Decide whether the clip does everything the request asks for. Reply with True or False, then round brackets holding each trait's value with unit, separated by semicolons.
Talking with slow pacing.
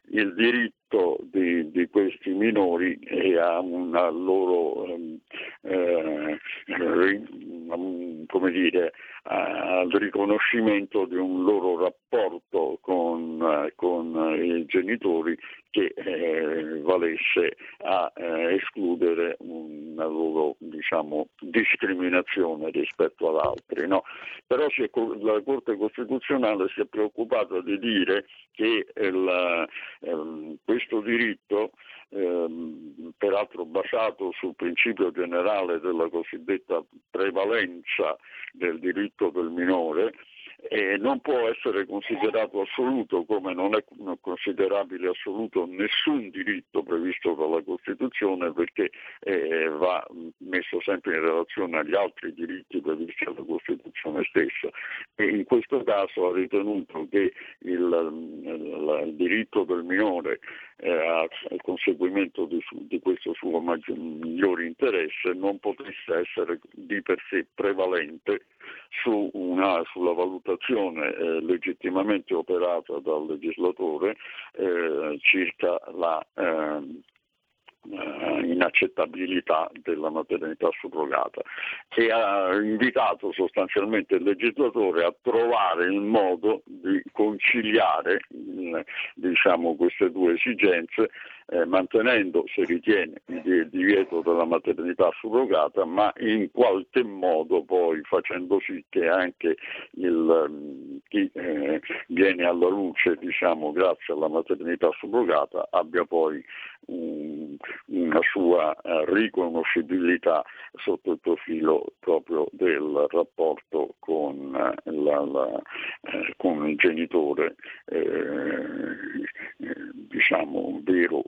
True (105 wpm)